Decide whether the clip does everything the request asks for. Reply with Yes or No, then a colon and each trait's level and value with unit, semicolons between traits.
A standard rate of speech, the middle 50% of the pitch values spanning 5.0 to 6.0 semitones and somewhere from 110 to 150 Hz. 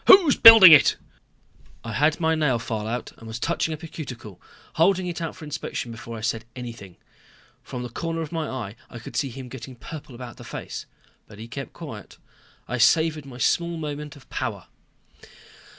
Yes: average, 190 wpm; wide, 5.5 semitones; low, 135 Hz